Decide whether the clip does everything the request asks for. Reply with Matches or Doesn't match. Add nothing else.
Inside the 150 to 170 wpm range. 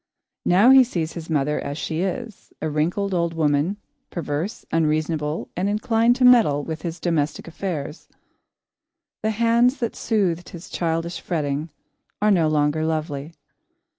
Doesn't match